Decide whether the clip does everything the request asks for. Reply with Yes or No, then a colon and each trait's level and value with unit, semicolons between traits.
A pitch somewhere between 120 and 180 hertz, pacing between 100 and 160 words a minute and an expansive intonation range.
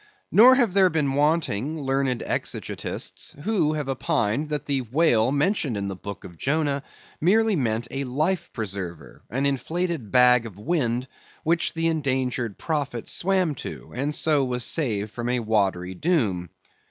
Yes: low, 135 Hz; average, 145 wpm; wide, 5.7 semitones